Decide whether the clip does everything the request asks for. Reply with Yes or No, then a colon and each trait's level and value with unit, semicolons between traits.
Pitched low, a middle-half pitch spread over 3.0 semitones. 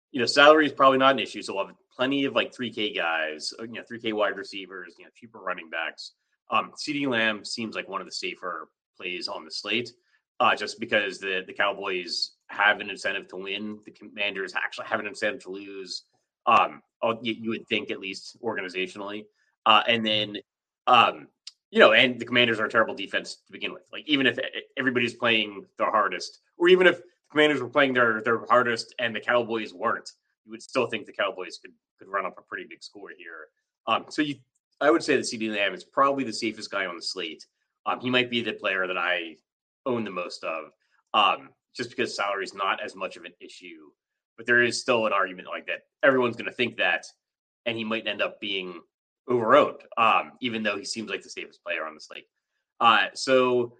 Yes: low, 115 Hz; average, 3.5 semitones